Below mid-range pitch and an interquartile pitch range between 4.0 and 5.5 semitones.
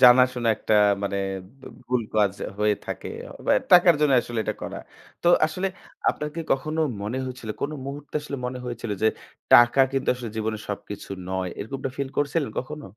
Yes: low, 125 Hz; average, 4.5 semitones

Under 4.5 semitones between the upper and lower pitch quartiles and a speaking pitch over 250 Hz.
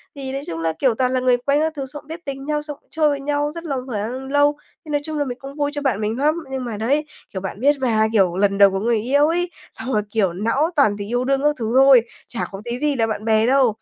No: average, 4.8 semitones; very high, 265 Hz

